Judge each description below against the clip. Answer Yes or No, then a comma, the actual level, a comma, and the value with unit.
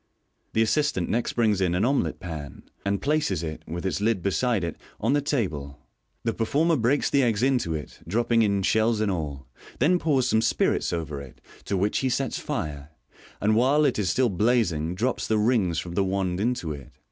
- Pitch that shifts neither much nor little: No, wide, 6.1 semitones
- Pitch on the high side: No, low, 105 Hz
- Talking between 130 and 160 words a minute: No, average, 200 wpm